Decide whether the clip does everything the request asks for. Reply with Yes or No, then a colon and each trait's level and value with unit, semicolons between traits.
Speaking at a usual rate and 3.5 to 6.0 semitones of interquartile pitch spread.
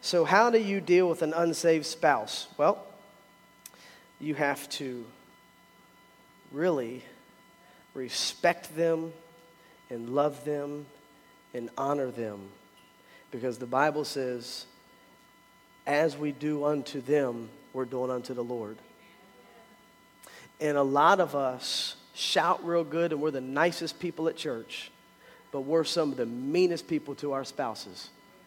No: slow, 130 wpm; average, 4.1 semitones